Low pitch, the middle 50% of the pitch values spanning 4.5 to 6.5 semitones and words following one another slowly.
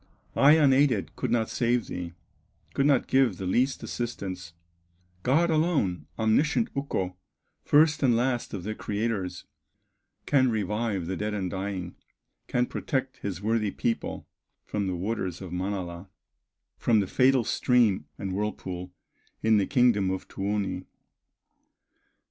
Yes: low, 105 Hz; average, 5.1 semitones; slow, 130 wpm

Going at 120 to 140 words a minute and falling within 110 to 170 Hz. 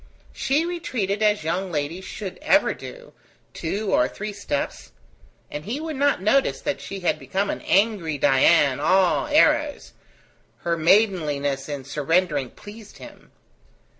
No: slow, 135 wpm; high, 190 Hz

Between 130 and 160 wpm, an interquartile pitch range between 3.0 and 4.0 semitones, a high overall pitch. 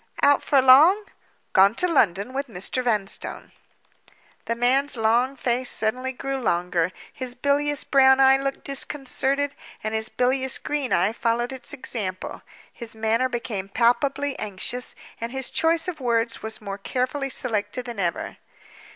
Yes: average, 145 wpm; average, 3.7 semitones; very high, 250 Hz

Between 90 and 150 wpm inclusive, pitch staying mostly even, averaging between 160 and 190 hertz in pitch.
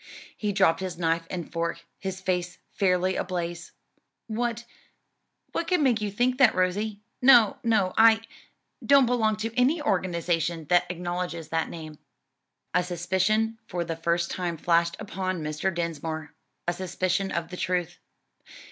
No: average, 145 wpm; average, 4.2 semitones; medium, 185 Hz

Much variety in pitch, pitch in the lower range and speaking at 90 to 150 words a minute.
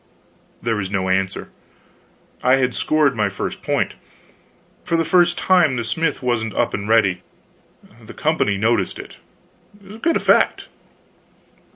Yes: wide, 7.2 semitones; low, 115 Hz; slow, 135 wpm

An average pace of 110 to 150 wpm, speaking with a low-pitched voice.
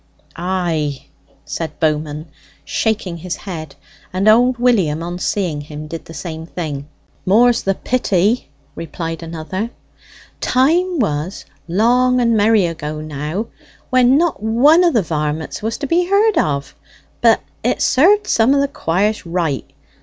No: average, 140 wpm; medium, 185 Hz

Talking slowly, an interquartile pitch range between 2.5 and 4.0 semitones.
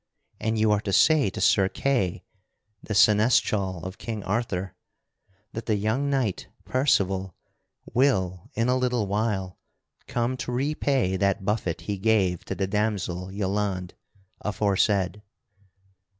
Yes: slow, 130 wpm; average, 3.4 semitones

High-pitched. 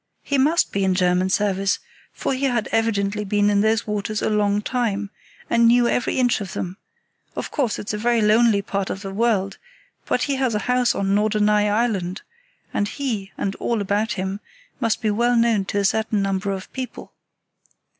Yes: high, 210 Hz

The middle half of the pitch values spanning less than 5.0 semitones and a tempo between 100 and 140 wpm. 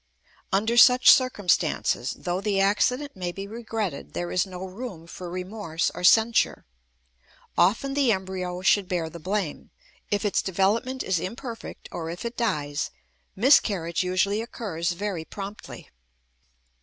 Yes: average, 4.0 semitones; slow, 135 wpm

